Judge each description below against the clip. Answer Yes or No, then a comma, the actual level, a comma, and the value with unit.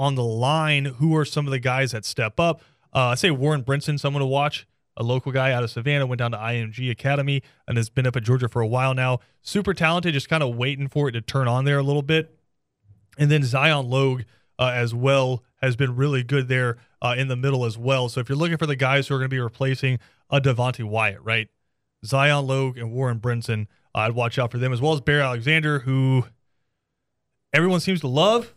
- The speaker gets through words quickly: Yes, fast, 235 wpm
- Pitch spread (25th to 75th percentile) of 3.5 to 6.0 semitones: No, average, 2.7 semitones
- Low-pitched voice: Yes, low, 130 Hz